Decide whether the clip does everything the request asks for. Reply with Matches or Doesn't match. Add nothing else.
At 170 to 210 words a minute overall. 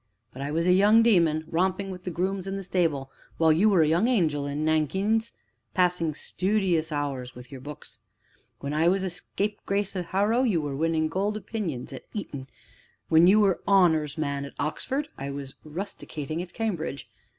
Matches